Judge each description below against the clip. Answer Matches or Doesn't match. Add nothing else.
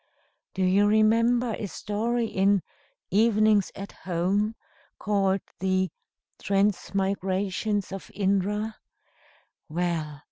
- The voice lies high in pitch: Matches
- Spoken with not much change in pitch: Matches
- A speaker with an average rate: Doesn't match